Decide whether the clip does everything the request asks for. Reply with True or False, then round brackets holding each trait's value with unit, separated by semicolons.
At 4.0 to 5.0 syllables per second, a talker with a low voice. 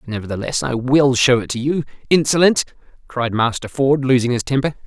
False (5.4 syllables/s; 130 Hz)